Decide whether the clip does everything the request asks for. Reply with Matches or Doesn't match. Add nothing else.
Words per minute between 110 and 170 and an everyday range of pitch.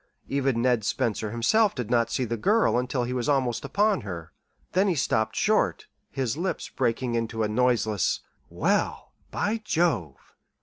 Matches